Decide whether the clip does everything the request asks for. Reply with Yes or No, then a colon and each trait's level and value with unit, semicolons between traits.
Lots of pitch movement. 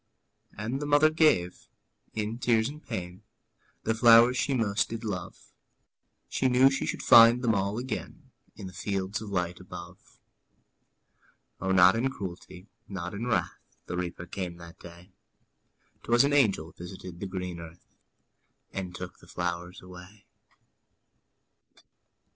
No: average, 4.6 semitones